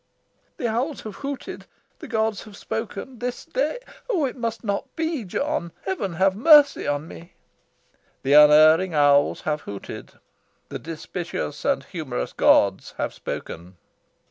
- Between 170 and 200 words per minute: No, average, 140 wpm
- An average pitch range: No, wide, 8.5 semitones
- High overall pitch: Yes, high, 200 Hz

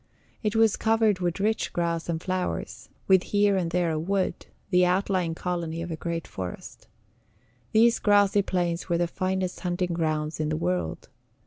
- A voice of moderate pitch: Yes, medium, 180 Hz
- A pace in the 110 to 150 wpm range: No, average, 165 wpm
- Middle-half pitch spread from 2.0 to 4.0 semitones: Yes, average, 2.8 semitones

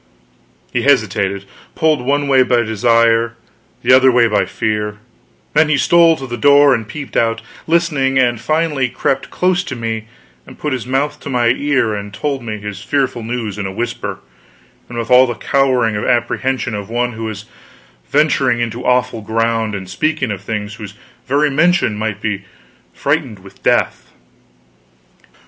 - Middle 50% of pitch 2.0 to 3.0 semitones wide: No, average, 4.0 semitones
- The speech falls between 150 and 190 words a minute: Yes, average, 165 wpm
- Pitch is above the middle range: No, low, 120 Hz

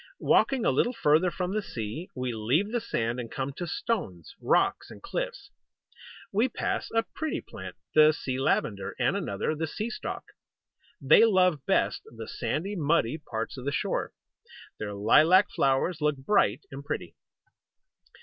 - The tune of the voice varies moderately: No, wide, 7.6 semitones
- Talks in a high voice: No, medium, 150 Hz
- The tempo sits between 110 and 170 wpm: Yes, average, 160 wpm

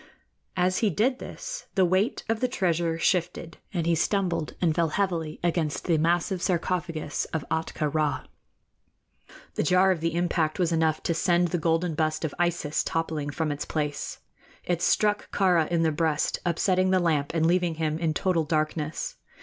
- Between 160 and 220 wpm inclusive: Yes, average, 175 wpm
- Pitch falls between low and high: Yes, medium, 170 Hz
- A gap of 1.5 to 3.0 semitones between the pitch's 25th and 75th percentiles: Yes, narrow, 2.4 semitones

